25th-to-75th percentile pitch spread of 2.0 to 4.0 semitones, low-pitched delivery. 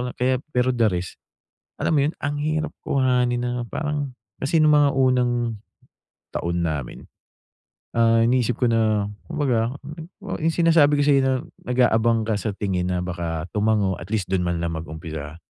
No: wide, 6.6 semitones; low, 115 Hz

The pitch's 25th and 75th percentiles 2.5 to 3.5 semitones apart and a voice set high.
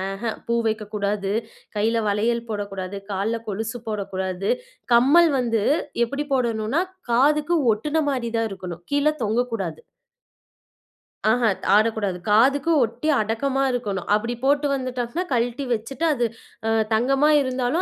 No: average, 4.2 semitones; high, 230 Hz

